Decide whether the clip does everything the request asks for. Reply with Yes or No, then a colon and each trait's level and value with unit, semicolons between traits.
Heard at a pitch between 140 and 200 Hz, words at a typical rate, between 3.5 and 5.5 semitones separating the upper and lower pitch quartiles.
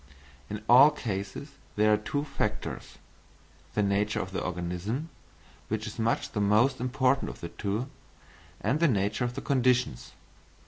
No: low, 110 Hz; average, 150 wpm; average, 4.5 semitones